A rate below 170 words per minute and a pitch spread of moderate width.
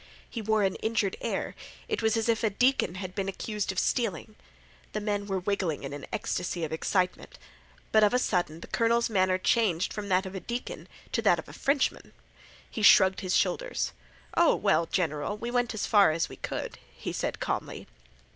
No: average, 195 wpm; average, 3.5 semitones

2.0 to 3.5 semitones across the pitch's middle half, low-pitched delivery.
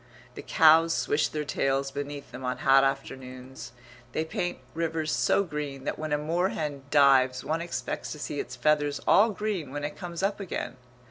No: average, 3.2 semitones; medium, 145 Hz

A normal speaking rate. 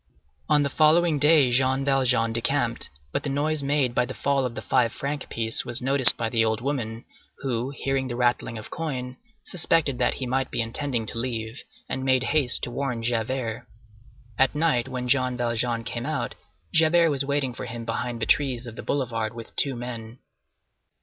Yes: average, 190 wpm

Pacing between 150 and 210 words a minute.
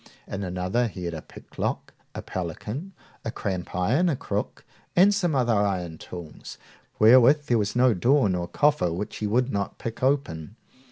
Yes: average, 165 wpm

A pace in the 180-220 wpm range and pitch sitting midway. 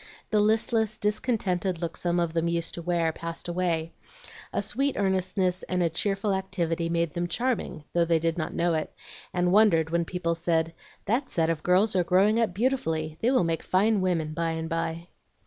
Yes: average, 190 wpm; medium, 175 Hz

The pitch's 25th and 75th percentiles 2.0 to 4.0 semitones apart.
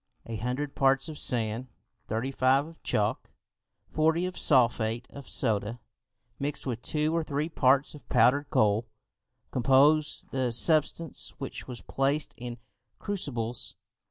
Yes: average, 3.7 semitones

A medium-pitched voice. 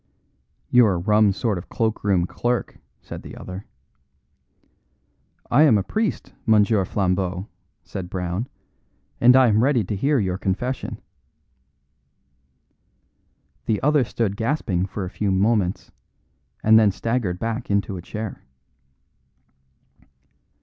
No: low, 105 Hz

